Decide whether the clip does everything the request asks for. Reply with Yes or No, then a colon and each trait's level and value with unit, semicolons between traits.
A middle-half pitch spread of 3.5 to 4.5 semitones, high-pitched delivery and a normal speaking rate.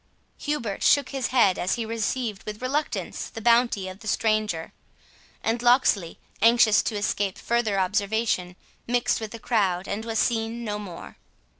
No: average, 2.8 semitones; high, 220 Hz; average, 155 wpm